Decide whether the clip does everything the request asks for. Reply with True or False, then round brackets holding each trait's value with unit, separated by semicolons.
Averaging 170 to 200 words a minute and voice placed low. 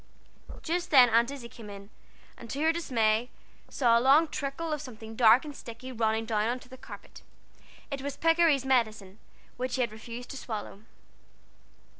False (175 wpm; 245 Hz)